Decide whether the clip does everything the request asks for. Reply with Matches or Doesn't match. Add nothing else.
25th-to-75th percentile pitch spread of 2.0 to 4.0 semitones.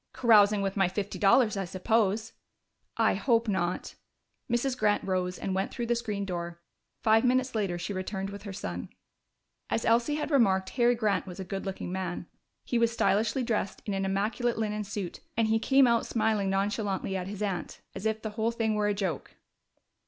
Matches